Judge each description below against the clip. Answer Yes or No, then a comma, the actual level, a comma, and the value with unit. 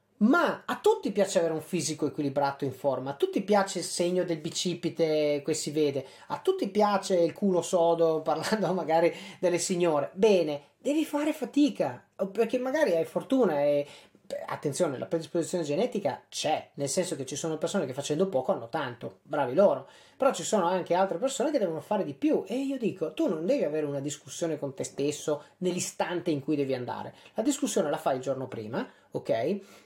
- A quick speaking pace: Yes, fast, 185 wpm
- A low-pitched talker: No, medium, 170 Hz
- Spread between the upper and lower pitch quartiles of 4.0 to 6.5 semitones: Yes, wide, 5.4 semitones